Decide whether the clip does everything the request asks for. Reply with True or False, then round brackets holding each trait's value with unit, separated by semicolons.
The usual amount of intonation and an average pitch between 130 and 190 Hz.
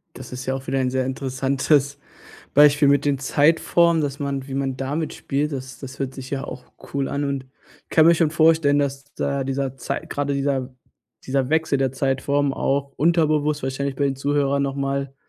False (1.3 semitones; 140 Hz)